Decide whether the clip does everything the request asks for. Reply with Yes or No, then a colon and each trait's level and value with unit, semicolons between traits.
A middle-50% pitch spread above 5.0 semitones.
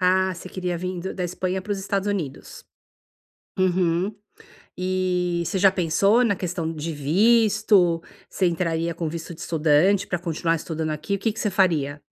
No: narrow, 2.6 semitones